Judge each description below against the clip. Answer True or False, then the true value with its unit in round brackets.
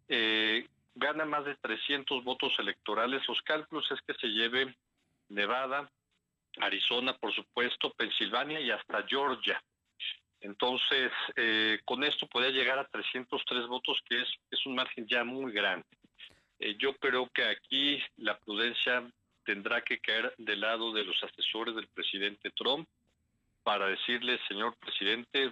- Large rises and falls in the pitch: False (3.5 semitones)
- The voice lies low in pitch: True (125 Hz)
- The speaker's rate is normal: True (140 wpm)